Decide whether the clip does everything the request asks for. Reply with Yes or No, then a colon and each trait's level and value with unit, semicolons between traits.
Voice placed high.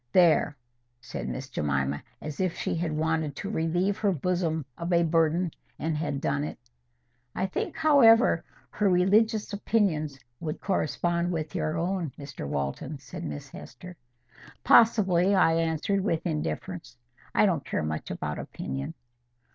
No: medium, 165 Hz